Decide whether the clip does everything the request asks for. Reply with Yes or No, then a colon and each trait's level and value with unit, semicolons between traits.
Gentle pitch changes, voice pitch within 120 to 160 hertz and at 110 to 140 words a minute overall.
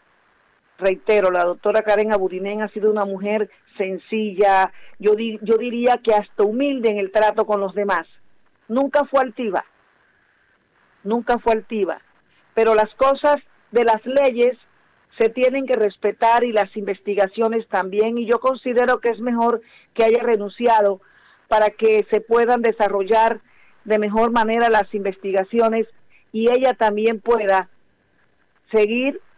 No: narrow, 2.3 semitones; high, 220 Hz; average, 135 wpm